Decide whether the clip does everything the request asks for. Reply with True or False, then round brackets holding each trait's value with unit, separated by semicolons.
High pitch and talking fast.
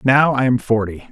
False (120 Hz; 215 wpm)